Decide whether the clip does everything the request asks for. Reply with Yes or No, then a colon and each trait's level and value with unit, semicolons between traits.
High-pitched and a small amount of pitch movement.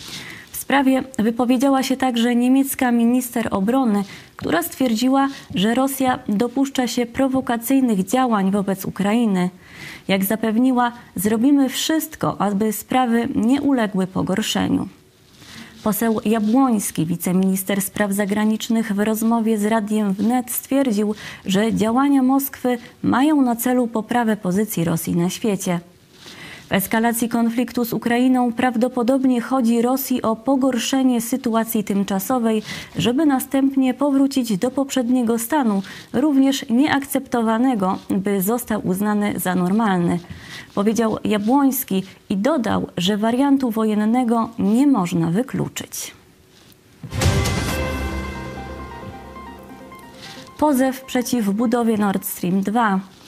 No: high, 230 Hz; average, 4.2 semitones